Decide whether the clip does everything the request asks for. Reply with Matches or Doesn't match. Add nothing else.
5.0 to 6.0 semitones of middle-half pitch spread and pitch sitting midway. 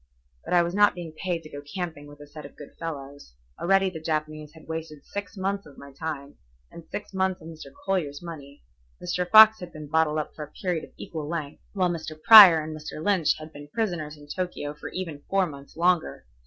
Doesn't match